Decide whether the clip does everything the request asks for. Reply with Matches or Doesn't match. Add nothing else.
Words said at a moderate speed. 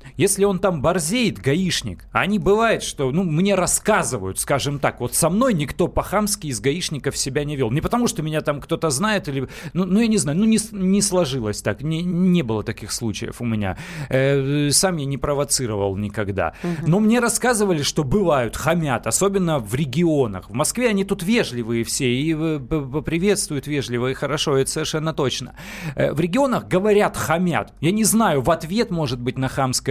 Doesn't match